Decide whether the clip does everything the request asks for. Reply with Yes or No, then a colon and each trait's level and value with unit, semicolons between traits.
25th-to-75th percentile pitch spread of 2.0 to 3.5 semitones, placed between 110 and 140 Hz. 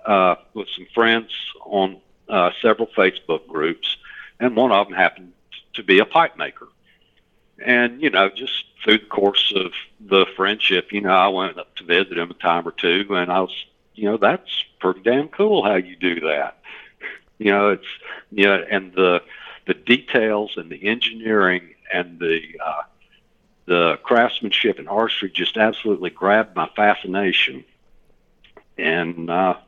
No: average, 3.2 semitones; low, 100 Hz